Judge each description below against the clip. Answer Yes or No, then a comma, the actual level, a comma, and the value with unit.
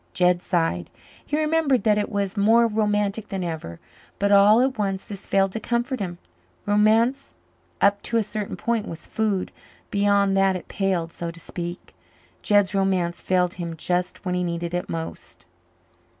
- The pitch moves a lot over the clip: No, average, 3.2 semitones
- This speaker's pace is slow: No, average, 165 wpm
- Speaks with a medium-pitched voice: No, high, 195 Hz